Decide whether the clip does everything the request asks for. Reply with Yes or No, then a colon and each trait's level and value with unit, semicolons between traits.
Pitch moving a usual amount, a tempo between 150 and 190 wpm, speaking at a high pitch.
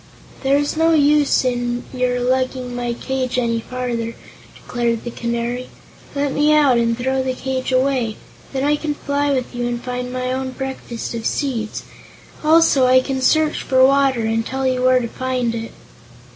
No: narrow, 1.9 semitones; average, 175 wpm; very high, 255 Hz